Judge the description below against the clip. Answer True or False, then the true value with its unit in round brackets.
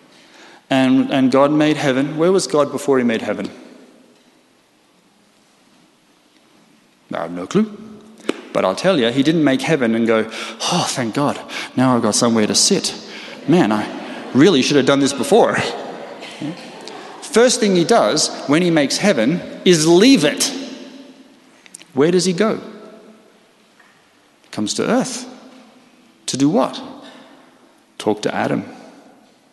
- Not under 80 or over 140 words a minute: True (135 wpm)